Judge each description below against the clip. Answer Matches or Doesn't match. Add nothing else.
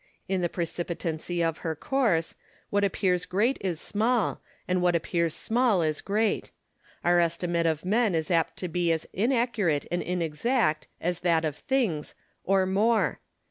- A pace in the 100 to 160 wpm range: Matches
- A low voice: Doesn't match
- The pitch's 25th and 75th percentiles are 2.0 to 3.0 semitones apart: Doesn't match